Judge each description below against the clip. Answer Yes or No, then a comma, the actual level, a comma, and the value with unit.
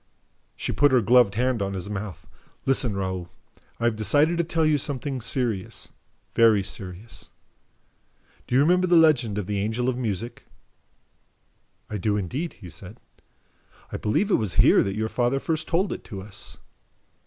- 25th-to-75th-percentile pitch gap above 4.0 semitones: Yes, wide, 5.4 semitones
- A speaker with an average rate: Yes, average, 165 wpm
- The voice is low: Yes, low, 115 Hz